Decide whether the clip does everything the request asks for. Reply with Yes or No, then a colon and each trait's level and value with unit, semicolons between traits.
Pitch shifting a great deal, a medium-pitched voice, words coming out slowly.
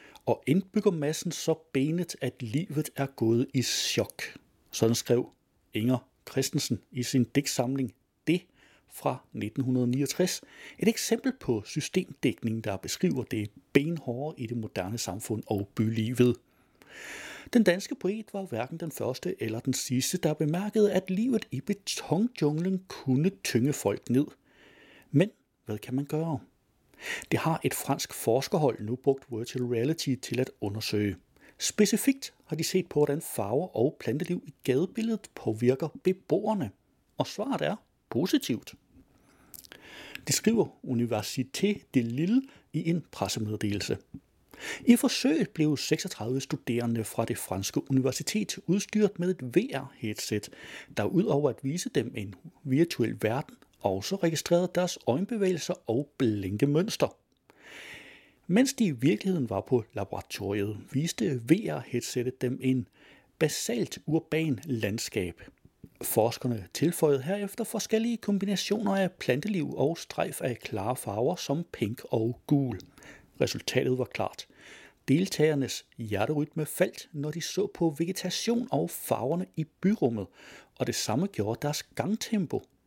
Yes: wide, 7.2 semitones; medium, 145 Hz; slow, 130 wpm